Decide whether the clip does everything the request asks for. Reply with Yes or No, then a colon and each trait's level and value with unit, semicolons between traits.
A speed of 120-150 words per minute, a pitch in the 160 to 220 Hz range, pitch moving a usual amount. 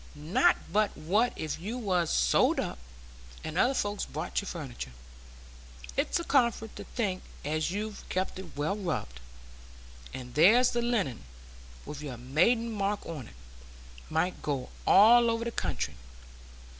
No: average, 145 wpm; medium, 185 Hz; wide, 6.9 semitones